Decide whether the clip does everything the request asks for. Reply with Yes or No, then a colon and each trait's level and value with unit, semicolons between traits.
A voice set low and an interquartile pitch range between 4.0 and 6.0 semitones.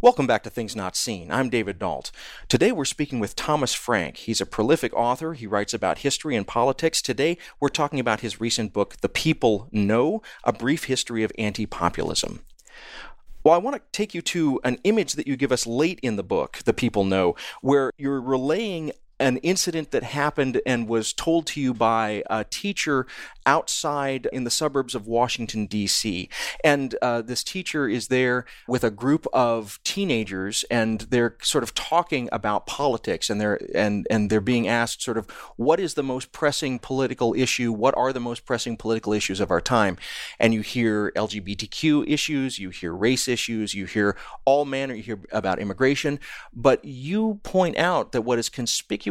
Yes: low, 125 Hz; average, 4.4 semitones